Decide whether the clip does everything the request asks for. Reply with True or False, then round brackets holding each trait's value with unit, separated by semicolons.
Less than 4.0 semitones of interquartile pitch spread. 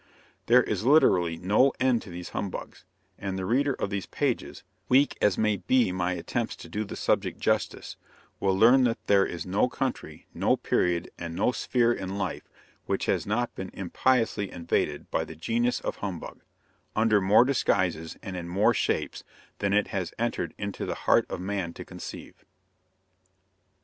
False (4.6 semitones)